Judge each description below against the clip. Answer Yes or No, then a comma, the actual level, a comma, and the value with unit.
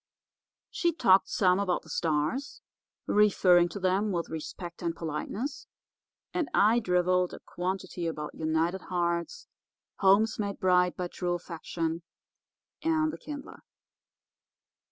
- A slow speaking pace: Yes, slow, 120 wpm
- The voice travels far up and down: No, average, 3.4 semitones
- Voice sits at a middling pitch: Yes, medium, 180 Hz